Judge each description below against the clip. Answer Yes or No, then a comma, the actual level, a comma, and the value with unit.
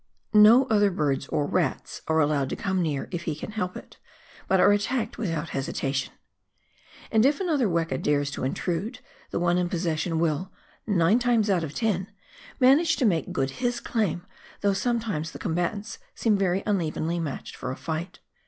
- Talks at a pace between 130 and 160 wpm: No, average, 185 wpm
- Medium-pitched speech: Yes, medium, 180 Hz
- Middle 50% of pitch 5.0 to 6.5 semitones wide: Yes, wide, 5.4 semitones